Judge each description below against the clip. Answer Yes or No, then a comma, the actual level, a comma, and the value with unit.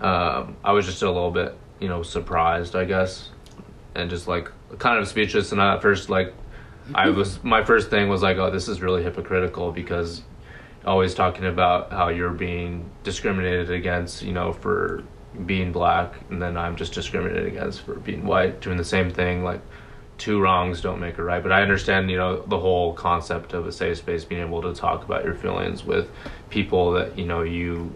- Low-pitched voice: Yes, very low, 90 Hz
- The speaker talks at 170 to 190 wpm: No, average, 200 wpm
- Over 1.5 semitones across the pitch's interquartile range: No, narrow, 1.2 semitones